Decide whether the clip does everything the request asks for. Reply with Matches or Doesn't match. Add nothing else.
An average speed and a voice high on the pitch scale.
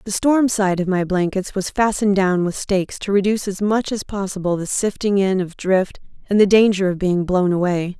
Doesn't match